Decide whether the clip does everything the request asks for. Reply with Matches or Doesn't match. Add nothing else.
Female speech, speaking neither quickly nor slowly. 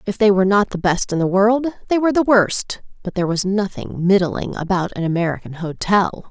Doesn't match